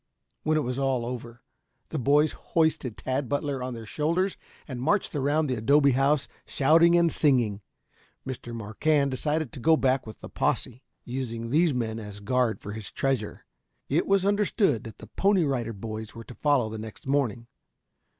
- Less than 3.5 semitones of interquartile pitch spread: No, average, 4.6 semitones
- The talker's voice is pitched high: No, low, 130 Hz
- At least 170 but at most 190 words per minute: Yes, average, 175 wpm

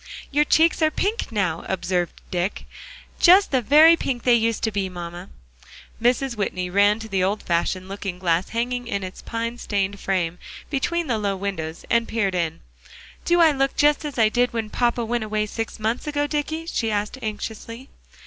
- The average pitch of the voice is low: No, high, 220 Hz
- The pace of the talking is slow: No, average, 185 wpm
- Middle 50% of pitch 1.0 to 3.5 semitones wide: No, wide, 5.4 semitones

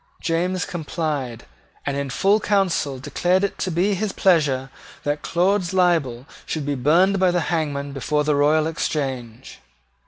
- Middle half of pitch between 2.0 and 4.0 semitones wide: No, average, 4.6 semitones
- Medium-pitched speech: Yes, medium, 160 Hz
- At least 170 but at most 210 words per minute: No, average, 150 wpm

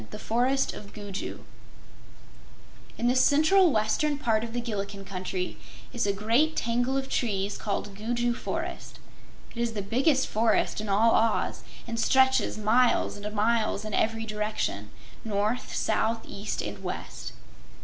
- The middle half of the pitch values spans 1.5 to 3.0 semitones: Yes, narrow, 2.6 semitones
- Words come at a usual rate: Yes, average, 150 wpm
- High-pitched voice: Yes, high, 225 Hz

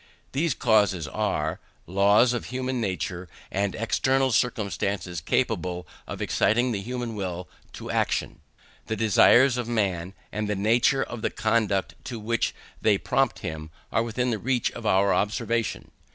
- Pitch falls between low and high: No, low, 110 Hz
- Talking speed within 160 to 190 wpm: No, average, 150 wpm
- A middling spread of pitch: Yes, average, 3.8 semitones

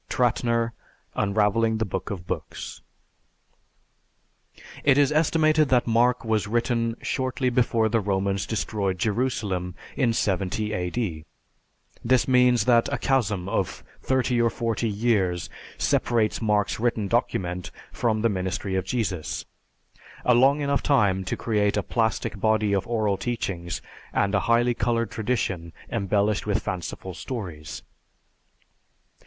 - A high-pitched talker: No, low, 110 Hz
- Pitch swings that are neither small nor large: Yes, average, 3.6 semitones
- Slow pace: Yes, slow, 125 wpm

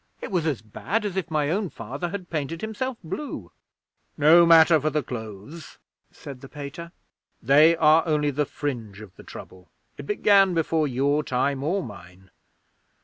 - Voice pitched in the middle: Yes, medium, 150 Hz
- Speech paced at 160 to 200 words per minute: Yes, average, 165 wpm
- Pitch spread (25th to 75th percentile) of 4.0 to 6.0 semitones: Yes, average, 4.4 semitones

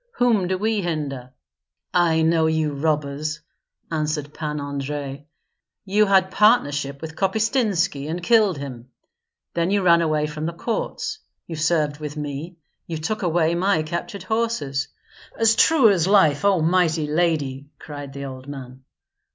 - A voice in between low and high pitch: Yes, medium, 160 Hz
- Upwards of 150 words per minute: No, average, 145 wpm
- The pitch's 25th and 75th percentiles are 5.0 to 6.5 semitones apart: No, average, 4.5 semitones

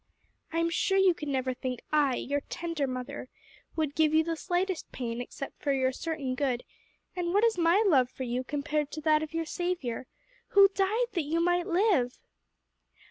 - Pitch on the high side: Yes, very high, 310 Hz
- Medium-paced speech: Yes, average, 190 wpm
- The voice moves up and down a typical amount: Yes, average, 5.0 semitones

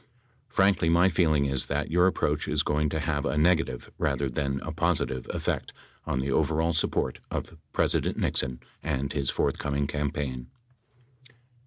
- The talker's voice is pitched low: Yes, very low, 75 Hz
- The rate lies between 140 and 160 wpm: Yes, average, 150 wpm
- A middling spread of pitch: Yes, average, 3.1 semitones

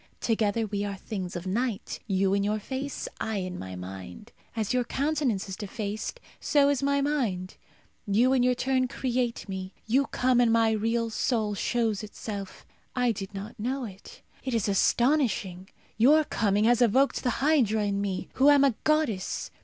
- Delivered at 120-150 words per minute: No, average, 175 wpm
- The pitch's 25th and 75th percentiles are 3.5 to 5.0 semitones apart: Yes, average, 4.4 semitones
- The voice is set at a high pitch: Yes, high, 225 Hz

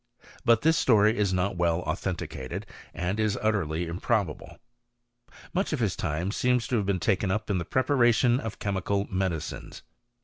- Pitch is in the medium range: No, low, 100 Hz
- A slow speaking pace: No, average, 160 wpm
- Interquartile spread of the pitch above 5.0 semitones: No, average, 4.2 semitones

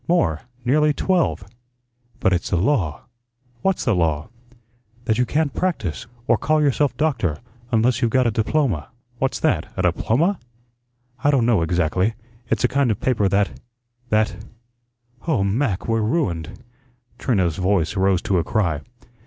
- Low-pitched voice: Yes, low, 110 Hz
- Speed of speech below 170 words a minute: Yes, average, 150 wpm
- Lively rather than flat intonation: Yes, wide, 7.5 semitones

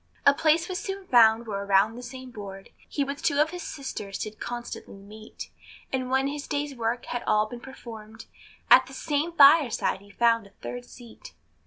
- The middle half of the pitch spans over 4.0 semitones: Yes, average, 4.8 semitones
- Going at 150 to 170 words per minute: No, average, 190 wpm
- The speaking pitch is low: No, high, 245 Hz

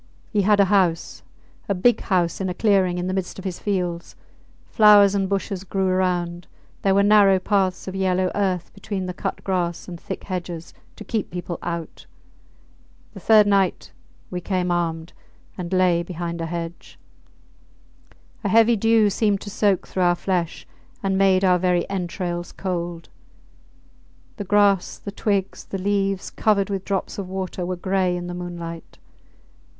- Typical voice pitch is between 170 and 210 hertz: Yes, medium, 185 Hz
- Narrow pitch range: Yes, narrow, 2.1 semitones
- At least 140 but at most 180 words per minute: Yes, average, 165 wpm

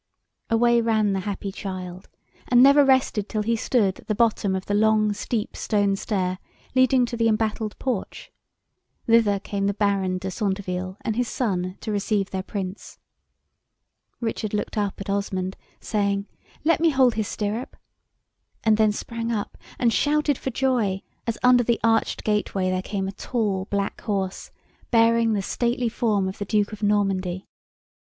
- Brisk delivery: No, average, 165 wpm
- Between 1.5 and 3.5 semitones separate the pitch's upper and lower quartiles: Yes, average, 2.9 semitones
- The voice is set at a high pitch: Yes, high, 210 Hz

